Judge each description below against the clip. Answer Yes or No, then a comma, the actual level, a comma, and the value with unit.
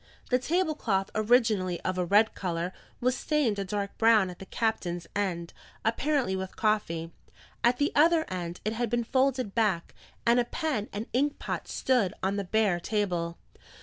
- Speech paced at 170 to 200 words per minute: Yes, average, 175 wpm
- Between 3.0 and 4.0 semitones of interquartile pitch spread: No, average, 4.8 semitones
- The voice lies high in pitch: Yes, high, 215 Hz